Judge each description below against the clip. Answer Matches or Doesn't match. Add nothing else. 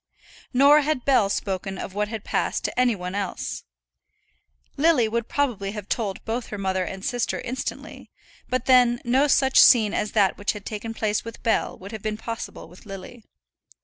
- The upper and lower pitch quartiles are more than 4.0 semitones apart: Doesn't match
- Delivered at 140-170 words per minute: Doesn't match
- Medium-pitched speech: Doesn't match